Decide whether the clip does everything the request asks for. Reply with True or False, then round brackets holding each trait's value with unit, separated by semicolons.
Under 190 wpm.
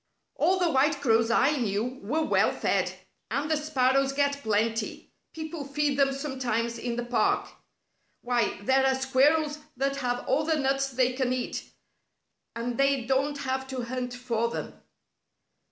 True (155 wpm)